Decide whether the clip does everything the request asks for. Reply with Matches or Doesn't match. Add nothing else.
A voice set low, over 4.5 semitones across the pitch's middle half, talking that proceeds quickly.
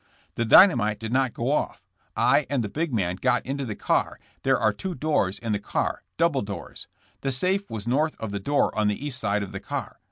Matches